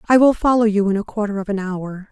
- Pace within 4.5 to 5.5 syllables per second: No, 6.0 syllables/s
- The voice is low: No, high, 210 Hz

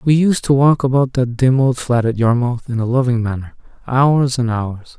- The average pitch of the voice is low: Yes, low, 125 Hz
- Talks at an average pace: No, fast, 215 wpm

